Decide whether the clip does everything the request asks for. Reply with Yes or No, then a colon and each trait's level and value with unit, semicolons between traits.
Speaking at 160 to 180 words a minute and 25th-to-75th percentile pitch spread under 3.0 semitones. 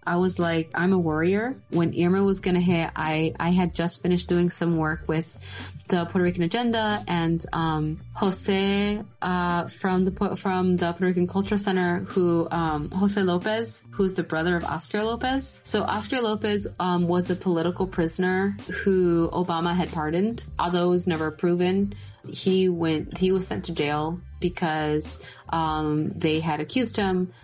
Yes: average, 165 wpm; narrow, 2.6 semitones